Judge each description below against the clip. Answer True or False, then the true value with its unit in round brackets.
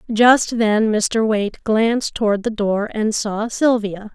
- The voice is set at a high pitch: True (220 Hz)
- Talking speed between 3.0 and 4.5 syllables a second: True (3.8 syllables/s)